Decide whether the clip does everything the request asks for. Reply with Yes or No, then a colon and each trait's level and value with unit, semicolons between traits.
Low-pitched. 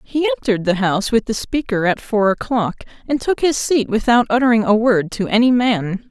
No: high, 230 Hz